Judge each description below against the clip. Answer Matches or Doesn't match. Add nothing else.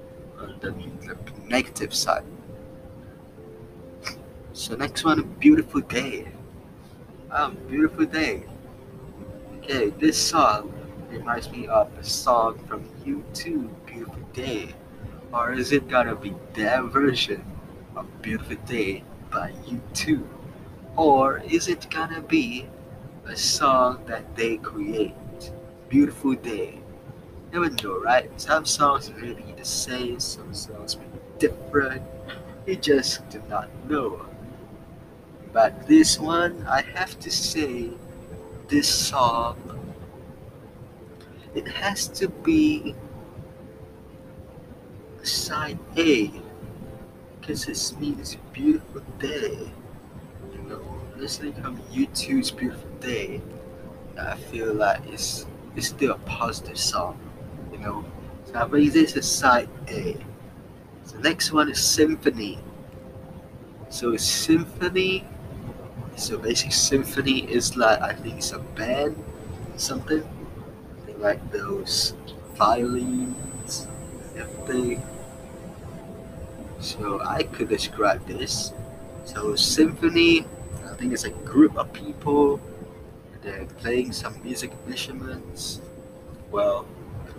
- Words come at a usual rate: Doesn't match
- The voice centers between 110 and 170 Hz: Matches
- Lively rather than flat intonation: Matches